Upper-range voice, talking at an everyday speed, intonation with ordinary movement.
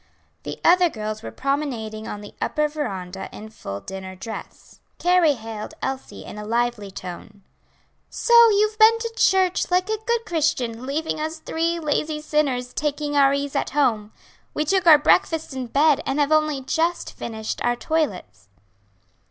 No: very high, 285 Hz; average, 160 wpm; wide, 6.5 semitones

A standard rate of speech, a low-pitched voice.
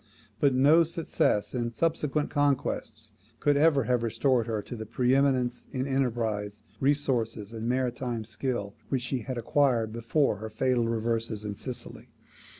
Yes: average, 150 wpm; low, 120 Hz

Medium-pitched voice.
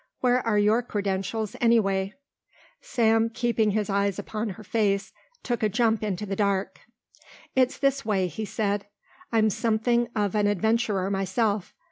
No: high, 215 Hz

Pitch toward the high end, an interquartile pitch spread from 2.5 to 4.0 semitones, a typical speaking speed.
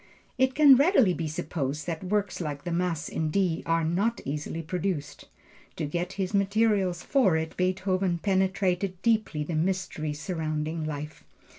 No: medium, 180 Hz; average, 3.7 semitones; average, 150 wpm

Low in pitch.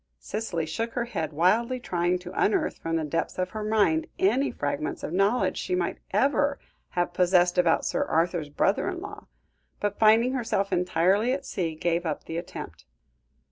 No: medium, 185 Hz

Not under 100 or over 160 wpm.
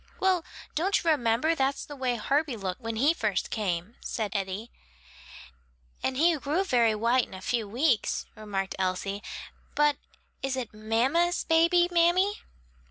Yes: average, 150 wpm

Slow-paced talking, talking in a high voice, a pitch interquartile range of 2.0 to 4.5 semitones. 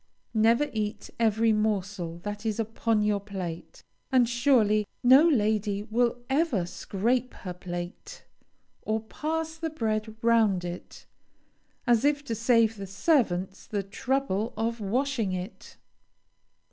Yes: slow, 125 wpm; high, 220 Hz; average, 3.4 semitones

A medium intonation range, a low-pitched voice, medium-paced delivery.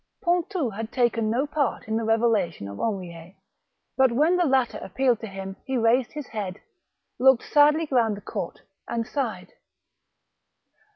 No: average, 4.2 semitones; high, 235 Hz; average, 155 wpm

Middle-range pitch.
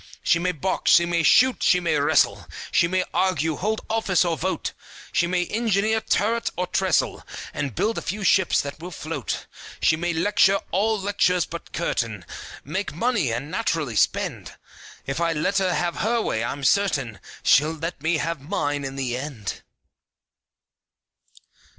Yes: medium, 170 Hz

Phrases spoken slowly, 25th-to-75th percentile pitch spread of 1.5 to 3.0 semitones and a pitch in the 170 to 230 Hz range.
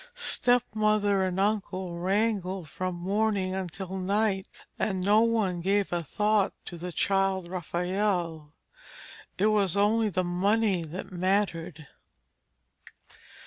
Yes: slow, 110 wpm; narrow, 2.6 semitones; high, 190 Hz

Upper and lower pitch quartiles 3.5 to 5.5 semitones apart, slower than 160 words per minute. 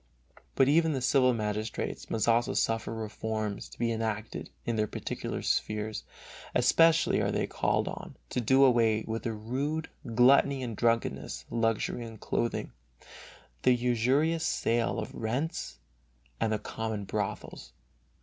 No: average, 2.8 semitones; average, 140 wpm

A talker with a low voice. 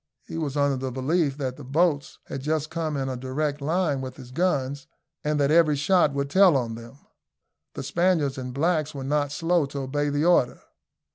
No: medium, 145 Hz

